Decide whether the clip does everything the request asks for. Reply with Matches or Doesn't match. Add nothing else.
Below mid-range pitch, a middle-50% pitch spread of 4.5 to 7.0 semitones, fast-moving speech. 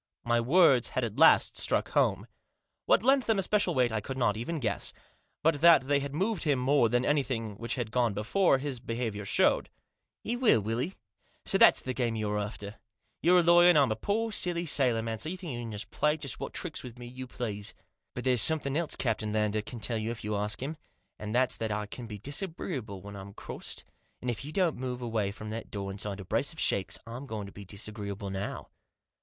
Matches